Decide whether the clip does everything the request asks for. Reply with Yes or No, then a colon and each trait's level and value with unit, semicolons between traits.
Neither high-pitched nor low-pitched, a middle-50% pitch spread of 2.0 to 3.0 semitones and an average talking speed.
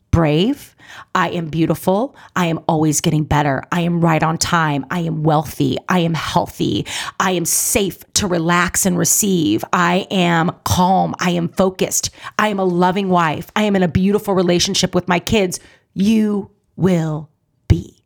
Yes: medium, 175 Hz; average, 2.7 semitones; average, 165 wpm